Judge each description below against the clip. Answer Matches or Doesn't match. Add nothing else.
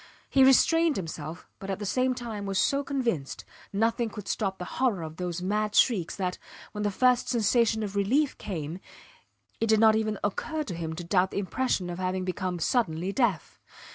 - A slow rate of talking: Doesn't match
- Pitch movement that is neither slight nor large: Matches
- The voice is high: Matches